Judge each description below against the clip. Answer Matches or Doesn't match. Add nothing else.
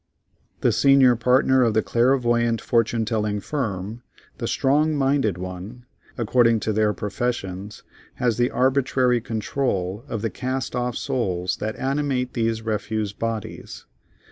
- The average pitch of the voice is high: Doesn't match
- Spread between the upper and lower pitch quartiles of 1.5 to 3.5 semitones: Matches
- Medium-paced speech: Doesn't match